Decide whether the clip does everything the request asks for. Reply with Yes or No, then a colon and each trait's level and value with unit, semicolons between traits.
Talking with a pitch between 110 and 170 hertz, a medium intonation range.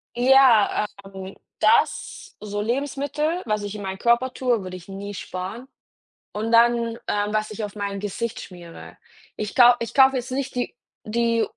No: high, 220 Hz; average, 3.4 semitones